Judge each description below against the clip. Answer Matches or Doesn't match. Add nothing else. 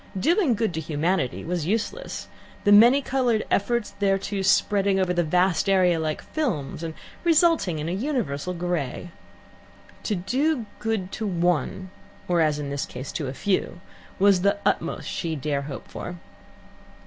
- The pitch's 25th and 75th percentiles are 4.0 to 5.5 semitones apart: Matches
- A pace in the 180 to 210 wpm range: Doesn't match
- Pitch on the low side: Doesn't match